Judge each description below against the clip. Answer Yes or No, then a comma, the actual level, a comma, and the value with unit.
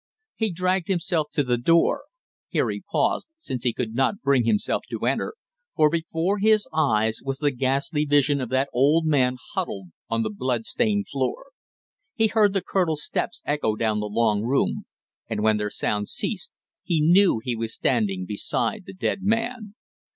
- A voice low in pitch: No, medium, 145 Hz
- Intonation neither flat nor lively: No, wide, 8.1 semitones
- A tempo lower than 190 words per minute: Yes, average, 175 wpm